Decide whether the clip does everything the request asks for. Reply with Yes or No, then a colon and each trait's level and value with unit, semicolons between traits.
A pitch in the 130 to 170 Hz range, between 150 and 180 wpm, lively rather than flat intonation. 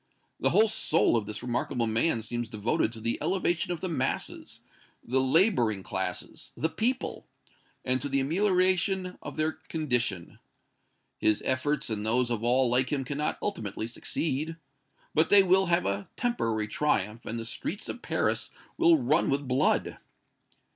Yes: low, 135 Hz; average, 155 wpm; wide, 7.1 semitones